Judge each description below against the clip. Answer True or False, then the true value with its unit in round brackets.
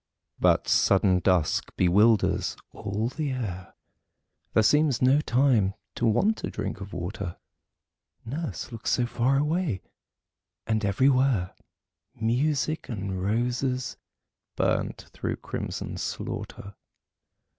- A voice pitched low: True (115 Hz)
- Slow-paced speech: True (105 wpm)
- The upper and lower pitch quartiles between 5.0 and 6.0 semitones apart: True (5.4 semitones)